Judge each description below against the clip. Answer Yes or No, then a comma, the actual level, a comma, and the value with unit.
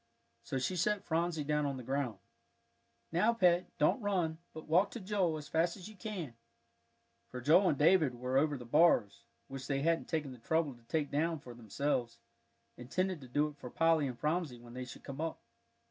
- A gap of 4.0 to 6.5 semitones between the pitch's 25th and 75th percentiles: Yes, average, 4.6 semitones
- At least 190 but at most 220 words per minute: Yes, average, 200 wpm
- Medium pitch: Yes, medium, 150 Hz